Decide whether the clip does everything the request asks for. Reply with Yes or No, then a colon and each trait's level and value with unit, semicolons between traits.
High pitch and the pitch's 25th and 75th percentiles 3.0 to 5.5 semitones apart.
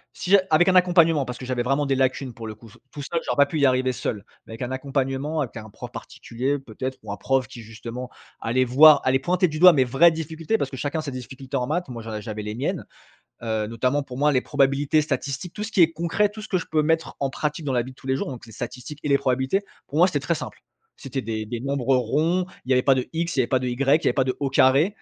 No: low, 135 Hz; average, 3.6 semitones